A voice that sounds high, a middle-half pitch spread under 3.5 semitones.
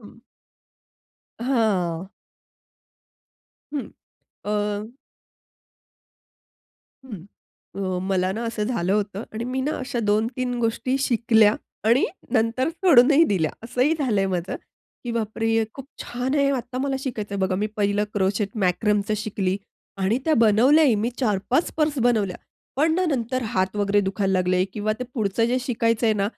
No: high, 225 Hz; average, 4.0 semitones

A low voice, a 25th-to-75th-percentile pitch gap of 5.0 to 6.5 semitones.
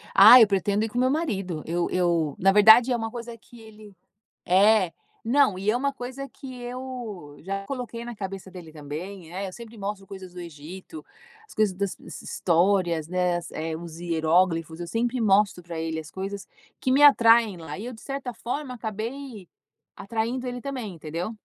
No: high, 200 Hz; wide, 5.4 semitones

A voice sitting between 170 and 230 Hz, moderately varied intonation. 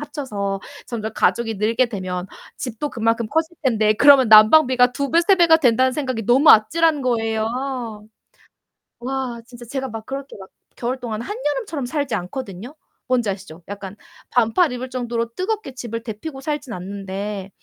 No: high, 245 Hz; average, 4.2 semitones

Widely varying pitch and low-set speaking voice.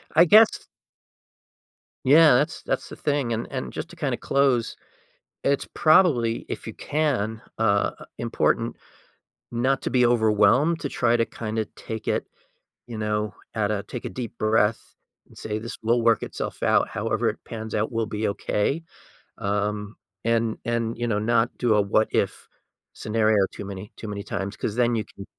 No: narrow, 2.5 semitones; low, 115 Hz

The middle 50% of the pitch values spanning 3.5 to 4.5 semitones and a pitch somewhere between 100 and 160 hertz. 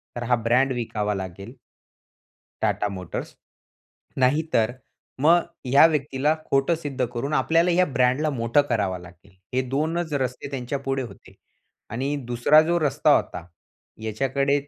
Yes: average, 3.9 semitones; low, 135 Hz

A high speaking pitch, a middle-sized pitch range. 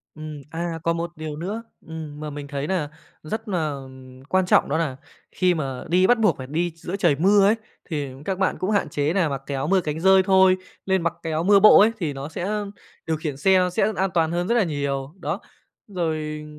No: medium, 165 Hz; average, 4.3 semitones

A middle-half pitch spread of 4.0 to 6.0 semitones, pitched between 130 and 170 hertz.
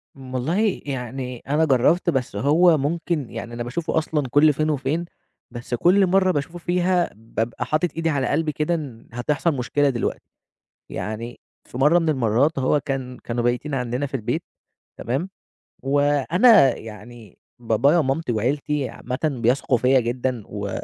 Yes: average, 4.5 semitones; low, 135 Hz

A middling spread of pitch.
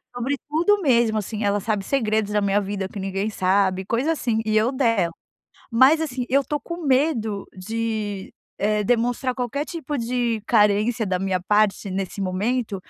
Yes: average, 3.9 semitones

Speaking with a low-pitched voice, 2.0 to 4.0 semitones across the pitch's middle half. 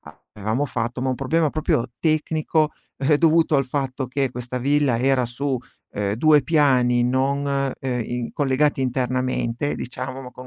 Yes: low, 130 Hz; average, 2.7 semitones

